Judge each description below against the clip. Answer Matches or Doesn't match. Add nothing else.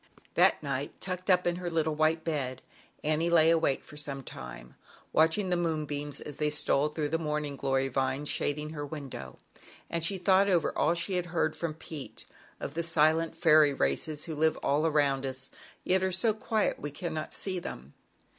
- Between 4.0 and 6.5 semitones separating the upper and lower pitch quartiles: Doesn't match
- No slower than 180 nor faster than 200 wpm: Matches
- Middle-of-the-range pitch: Matches